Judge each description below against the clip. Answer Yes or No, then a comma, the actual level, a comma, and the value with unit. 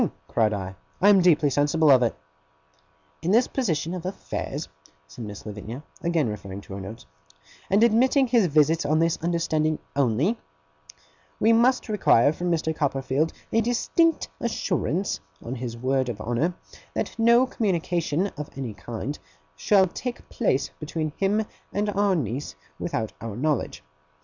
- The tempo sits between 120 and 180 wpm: Yes, average, 150 wpm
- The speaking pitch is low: No, medium, 155 Hz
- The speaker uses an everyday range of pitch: No, wide, 7.9 semitones